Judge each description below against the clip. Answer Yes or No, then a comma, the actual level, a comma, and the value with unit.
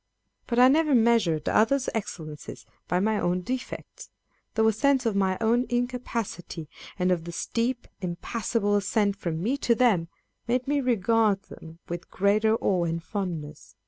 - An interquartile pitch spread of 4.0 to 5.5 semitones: Yes, average, 5.2 semitones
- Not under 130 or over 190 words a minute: Yes, average, 155 wpm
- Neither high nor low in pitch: No, high, 215 Hz